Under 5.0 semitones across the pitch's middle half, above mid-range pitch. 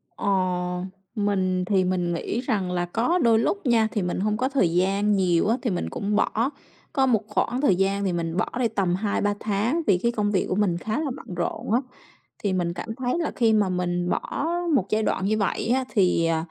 Yes: average, 4.1 semitones; high, 205 Hz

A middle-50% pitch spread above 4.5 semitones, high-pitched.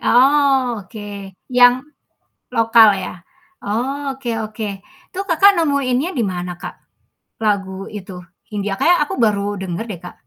Yes: average, 5.2 semitones; high, 225 Hz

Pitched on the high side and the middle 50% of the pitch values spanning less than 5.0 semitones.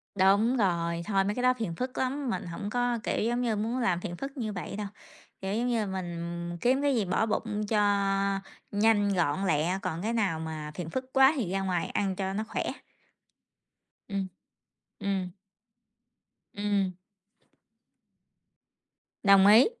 Yes: high, 205 Hz; average, 3.9 semitones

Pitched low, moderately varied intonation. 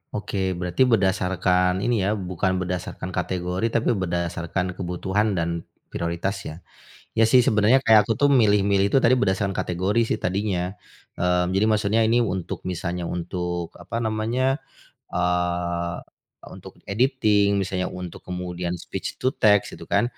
Yes: very low, 95 Hz; average, 3.2 semitones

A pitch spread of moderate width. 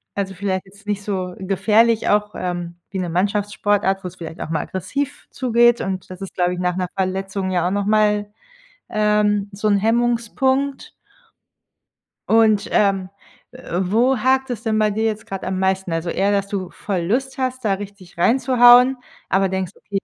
Yes: average, 3.0 semitones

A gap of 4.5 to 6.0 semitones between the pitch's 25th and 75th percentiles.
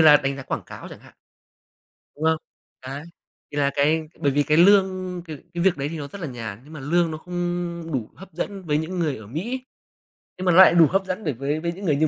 No: average, 3.8 semitones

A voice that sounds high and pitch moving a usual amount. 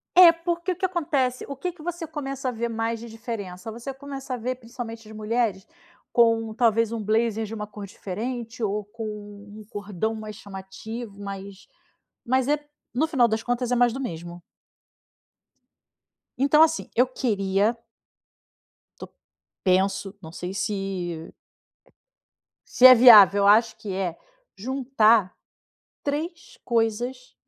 Yes: high, 225 Hz; average, 3.9 semitones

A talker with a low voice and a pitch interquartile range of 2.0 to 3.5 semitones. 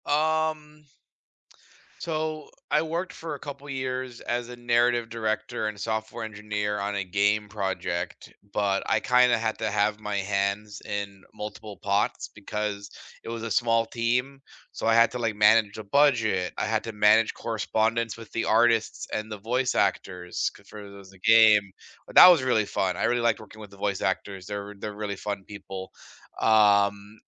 Yes: low, 110 Hz; average, 2.8 semitones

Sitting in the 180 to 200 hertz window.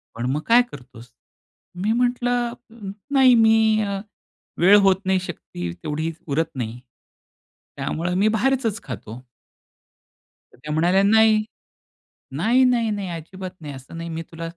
Yes: medium, 185 Hz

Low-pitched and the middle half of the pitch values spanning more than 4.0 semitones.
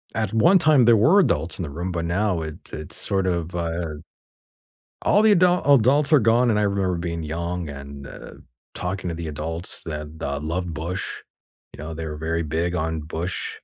Yes: very low, 85 Hz; average, 4.8 semitones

